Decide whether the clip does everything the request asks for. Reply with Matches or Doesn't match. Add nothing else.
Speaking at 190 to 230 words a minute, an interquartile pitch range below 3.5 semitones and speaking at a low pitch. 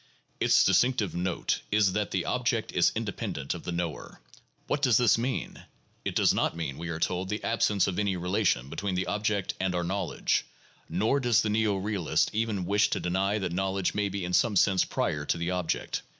Matches